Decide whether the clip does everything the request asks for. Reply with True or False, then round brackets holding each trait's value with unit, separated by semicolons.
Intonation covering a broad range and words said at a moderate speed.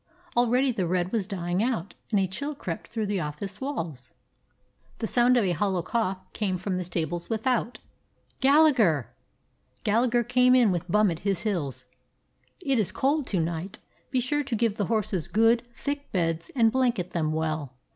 True (5.7 semitones; 175 wpm)